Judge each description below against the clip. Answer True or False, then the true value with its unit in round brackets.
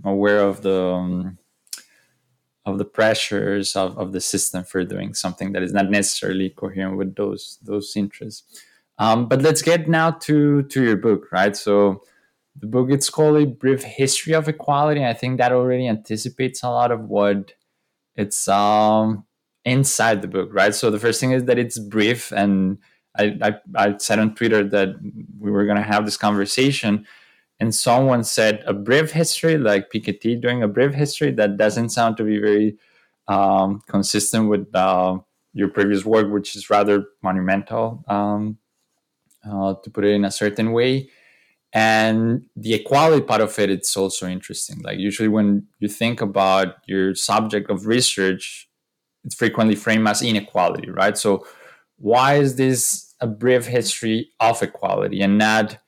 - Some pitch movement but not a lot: True (3.5 semitones)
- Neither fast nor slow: True (165 wpm)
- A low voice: True (105 Hz)